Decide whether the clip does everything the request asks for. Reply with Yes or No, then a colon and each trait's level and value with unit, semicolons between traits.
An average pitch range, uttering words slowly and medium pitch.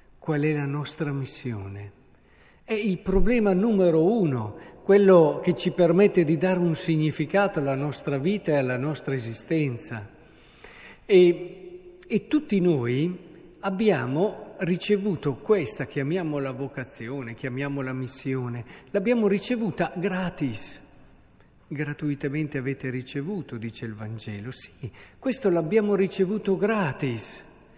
No: wide, 6.2 semitones; slow, 110 wpm; medium, 155 Hz